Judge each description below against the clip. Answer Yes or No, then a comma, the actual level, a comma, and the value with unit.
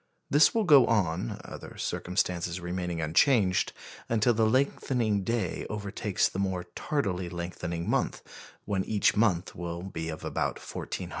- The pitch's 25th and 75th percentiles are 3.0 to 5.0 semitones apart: Yes, average, 4.3 semitones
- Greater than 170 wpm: No, average, 140 wpm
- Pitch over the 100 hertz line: No, very low, 95 Hz